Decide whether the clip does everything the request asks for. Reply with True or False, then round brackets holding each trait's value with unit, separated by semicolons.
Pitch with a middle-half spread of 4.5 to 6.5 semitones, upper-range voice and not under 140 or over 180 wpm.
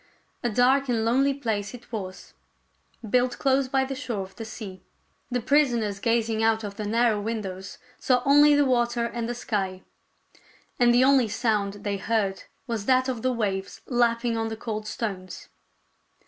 False (3.1 semitones; 230 Hz; 170 wpm)